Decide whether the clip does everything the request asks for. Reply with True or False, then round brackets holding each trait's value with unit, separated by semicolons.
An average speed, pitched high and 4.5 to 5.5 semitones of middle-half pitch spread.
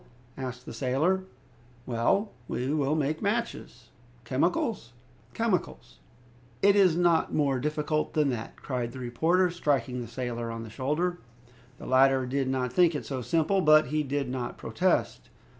False (150 wpm; 140 Hz; 5.0 semitones)